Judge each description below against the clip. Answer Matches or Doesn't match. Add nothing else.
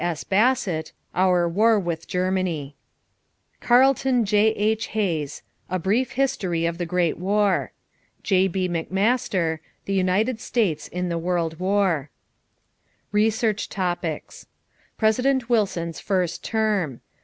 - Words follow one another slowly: Matches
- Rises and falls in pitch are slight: Doesn't match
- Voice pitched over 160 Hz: Matches